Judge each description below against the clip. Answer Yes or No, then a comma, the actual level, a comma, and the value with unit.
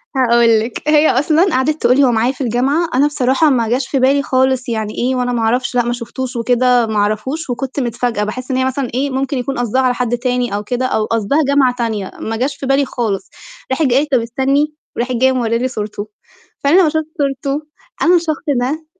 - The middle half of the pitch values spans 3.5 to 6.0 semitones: No, narrow, 2.6 semitones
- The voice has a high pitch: Yes, very high, 255 Hz